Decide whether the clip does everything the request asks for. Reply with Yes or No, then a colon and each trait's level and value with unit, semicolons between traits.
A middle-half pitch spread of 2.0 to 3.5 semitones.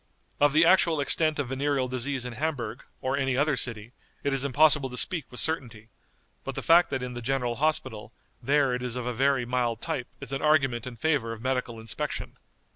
Yes: average, 3.0 semitones